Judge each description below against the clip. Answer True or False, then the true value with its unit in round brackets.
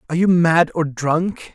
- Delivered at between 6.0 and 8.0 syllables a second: False (4.4 syllables/s)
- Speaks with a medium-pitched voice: True (165 Hz)